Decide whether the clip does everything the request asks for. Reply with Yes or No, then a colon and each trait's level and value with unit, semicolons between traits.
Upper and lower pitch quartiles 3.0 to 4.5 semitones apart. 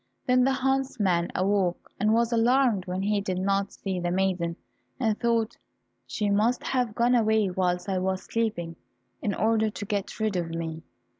Yes: average, 3.7 semitones